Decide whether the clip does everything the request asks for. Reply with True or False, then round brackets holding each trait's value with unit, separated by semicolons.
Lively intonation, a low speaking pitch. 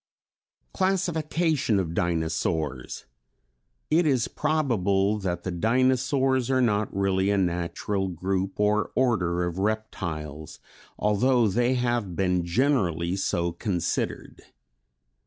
True (6.4 semitones; 100 Hz)